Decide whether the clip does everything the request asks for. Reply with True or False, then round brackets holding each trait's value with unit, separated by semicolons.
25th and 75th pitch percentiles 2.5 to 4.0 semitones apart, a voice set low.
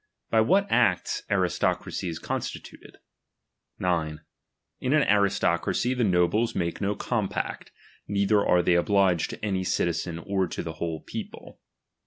True (3.4 semitones; 95 Hz)